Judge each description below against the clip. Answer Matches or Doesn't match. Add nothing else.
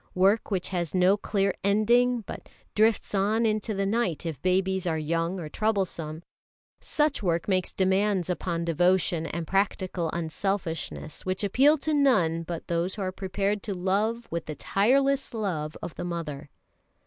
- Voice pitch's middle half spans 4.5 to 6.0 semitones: Doesn't match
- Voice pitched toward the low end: Doesn't match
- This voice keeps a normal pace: Matches